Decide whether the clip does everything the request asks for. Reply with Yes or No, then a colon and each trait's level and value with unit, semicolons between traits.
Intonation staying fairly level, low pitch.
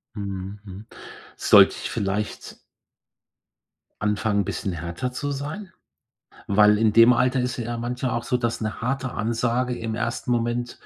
No: average, 3.2 semitones; low, 115 Hz